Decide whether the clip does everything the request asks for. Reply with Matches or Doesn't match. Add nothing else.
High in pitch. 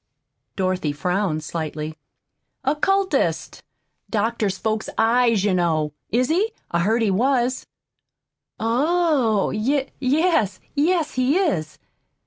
Matches